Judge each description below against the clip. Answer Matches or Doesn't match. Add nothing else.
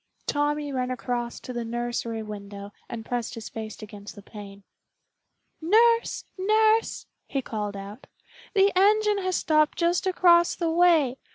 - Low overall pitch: Doesn't match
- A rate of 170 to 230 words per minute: Doesn't match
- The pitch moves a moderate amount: Doesn't match